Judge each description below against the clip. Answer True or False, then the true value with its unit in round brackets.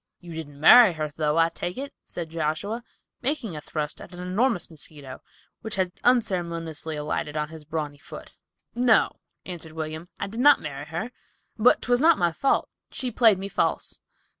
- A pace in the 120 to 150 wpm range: False (175 wpm)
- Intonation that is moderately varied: False (6.4 semitones)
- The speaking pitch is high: False (170 Hz)